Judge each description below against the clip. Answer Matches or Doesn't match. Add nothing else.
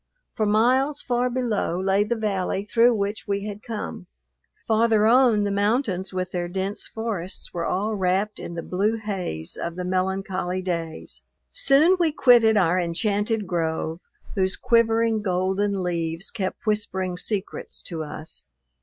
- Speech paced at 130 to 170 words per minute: Matches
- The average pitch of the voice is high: Matches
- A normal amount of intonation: Matches